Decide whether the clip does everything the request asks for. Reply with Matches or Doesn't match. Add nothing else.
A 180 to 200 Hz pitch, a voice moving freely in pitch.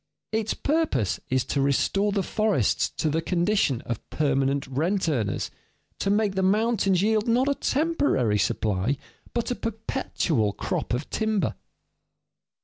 Matches